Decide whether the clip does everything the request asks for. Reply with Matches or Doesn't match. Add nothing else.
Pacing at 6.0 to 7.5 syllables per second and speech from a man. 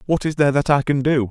Matches